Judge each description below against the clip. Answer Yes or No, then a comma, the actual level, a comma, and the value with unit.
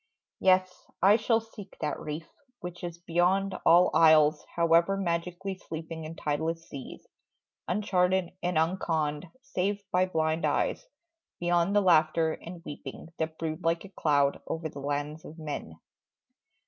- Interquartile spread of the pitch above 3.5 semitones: No, average, 2.7 semitones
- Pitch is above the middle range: No, medium, 170 Hz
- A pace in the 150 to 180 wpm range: No, average, 140 wpm